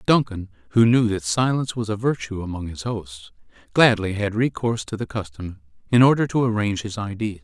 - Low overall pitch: Yes, low, 105 Hz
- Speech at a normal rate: Yes, average, 185 wpm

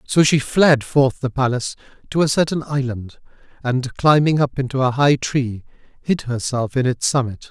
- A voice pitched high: No, low, 135 Hz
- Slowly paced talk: No, average, 175 wpm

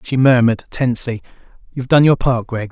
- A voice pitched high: No, low, 125 Hz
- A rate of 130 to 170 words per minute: No, average, 200 wpm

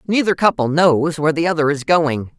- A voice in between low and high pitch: Yes, medium, 155 Hz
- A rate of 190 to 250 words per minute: Yes, average, 200 wpm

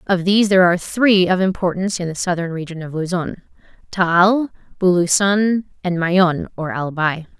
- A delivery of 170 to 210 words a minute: No, average, 145 wpm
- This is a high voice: No, medium, 180 Hz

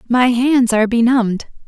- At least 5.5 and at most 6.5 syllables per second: No, 5.2 syllables/s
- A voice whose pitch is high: Yes, high, 240 Hz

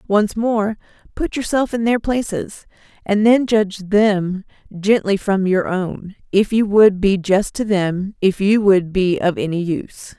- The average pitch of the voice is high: Yes, high, 200 Hz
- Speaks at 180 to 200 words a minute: No, average, 170 wpm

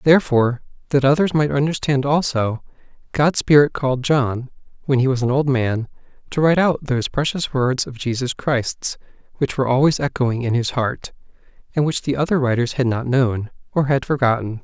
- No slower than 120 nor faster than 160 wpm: No, average, 175 wpm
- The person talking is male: Yes, male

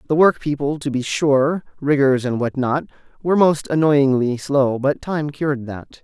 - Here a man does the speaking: Yes, male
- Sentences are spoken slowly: No, average, 150 wpm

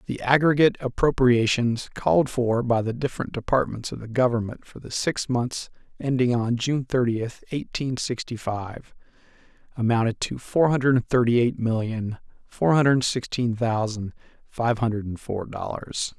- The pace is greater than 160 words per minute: No, average, 140 wpm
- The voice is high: No, low, 120 Hz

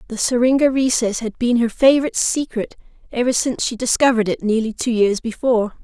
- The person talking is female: Yes, female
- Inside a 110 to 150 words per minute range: No, average, 175 wpm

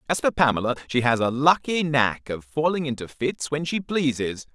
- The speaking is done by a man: Yes, male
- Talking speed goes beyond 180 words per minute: Yes, average, 200 wpm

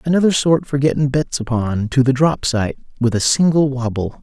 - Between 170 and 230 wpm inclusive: Yes, average, 200 wpm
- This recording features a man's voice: Yes, male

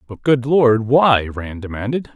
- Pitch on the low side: Yes, low, 120 Hz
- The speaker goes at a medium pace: Yes, average, 165 wpm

